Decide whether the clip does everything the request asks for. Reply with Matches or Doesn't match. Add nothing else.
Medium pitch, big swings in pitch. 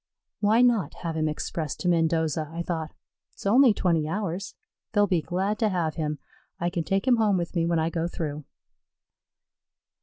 Doesn't match